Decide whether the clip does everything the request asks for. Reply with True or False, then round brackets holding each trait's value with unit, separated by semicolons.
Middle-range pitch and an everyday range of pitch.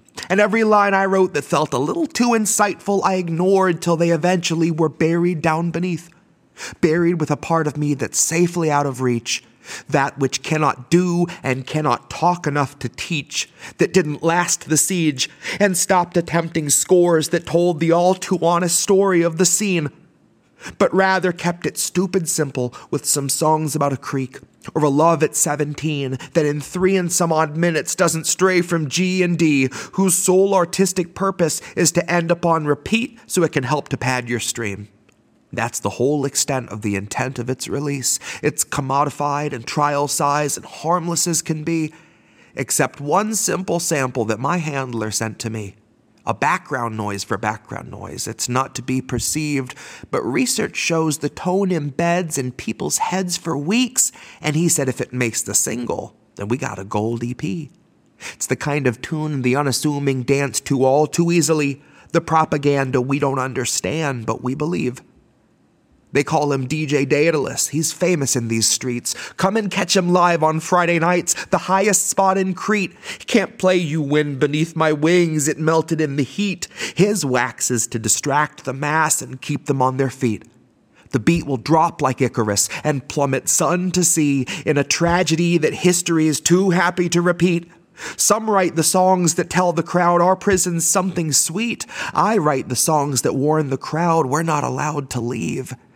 True (155 Hz; 4.3 semitones)